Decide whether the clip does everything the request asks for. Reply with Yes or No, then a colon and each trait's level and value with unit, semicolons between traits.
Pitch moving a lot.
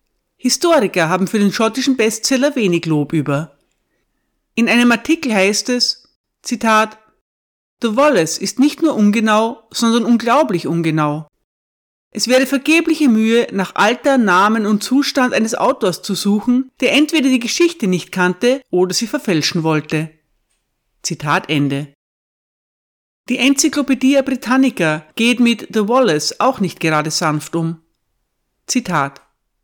Yes: wide, 7.4 semitones